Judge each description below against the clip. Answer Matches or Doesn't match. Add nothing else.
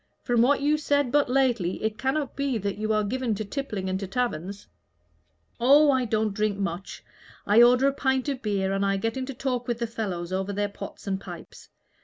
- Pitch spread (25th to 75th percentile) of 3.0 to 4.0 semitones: Doesn't match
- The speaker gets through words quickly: Matches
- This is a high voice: Matches